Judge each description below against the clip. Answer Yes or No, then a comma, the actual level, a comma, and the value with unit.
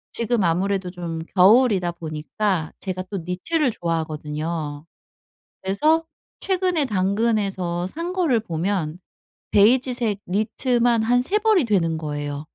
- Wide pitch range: Yes, wide, 6.3 semitones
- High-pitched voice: Yes, high, 195 Hz